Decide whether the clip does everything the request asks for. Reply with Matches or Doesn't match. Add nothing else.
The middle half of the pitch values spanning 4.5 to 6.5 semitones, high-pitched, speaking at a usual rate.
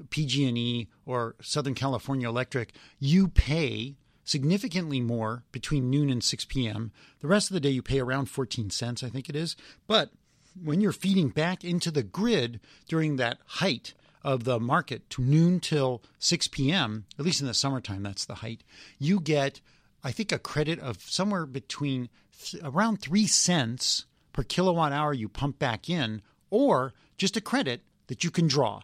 Doesn't match